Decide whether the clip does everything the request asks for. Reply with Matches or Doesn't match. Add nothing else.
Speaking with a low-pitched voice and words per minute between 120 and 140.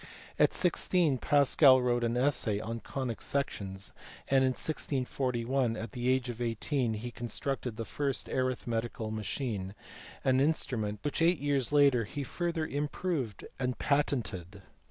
Matches